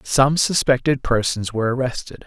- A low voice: Yes, low, 130 Hz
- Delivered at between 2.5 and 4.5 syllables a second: No, 5.1 syllables/s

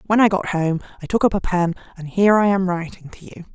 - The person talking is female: Yes, female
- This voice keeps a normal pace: No, fast, 270 wpm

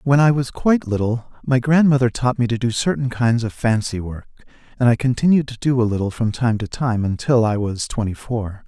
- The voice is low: Yes, low, 120 Hz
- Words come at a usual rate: No, fast, 220 wpm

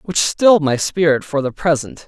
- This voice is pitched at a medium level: Yes, medium, 155 Hz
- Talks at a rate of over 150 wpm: Yes, fast, 205 wpm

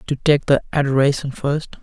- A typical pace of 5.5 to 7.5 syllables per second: No, 5.0 syllables/s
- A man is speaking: Yes, male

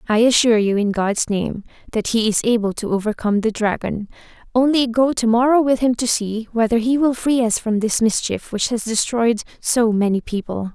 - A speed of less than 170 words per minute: No, average, 200 wpm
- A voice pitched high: Yes, high, 225 Hz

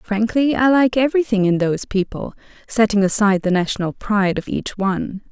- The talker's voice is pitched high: Yes, high, 210 Hz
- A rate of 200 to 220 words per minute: No, average, 170 wpm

